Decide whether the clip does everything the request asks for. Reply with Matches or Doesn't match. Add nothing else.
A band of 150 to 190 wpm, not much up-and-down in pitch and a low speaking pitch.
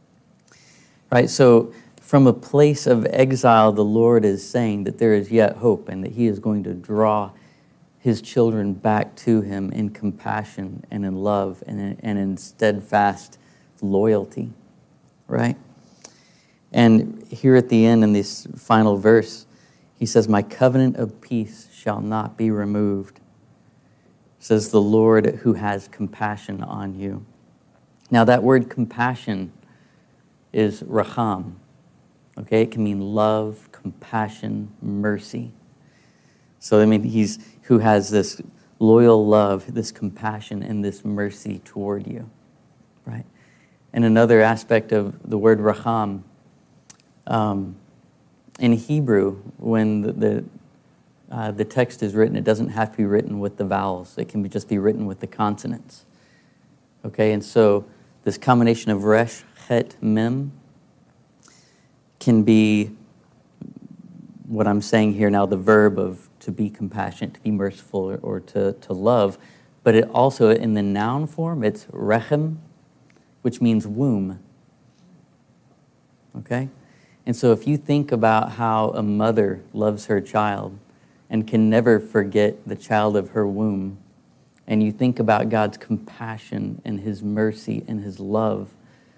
Doesn't match